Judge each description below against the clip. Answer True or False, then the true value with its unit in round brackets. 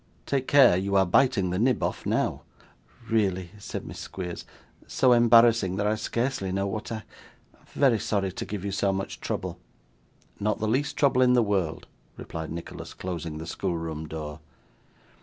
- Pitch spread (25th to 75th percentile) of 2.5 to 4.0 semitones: False (4.7 semitones)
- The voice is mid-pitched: False (100 Hz)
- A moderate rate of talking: True (165 wpm)